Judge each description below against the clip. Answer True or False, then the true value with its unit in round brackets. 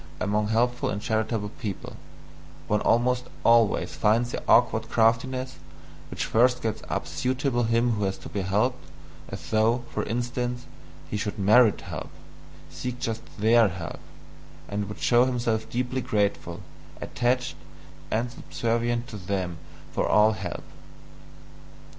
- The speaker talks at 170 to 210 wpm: False (135 wpm)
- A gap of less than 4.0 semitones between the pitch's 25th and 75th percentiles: True (2.7 semitones)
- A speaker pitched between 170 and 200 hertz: False (115 Hz)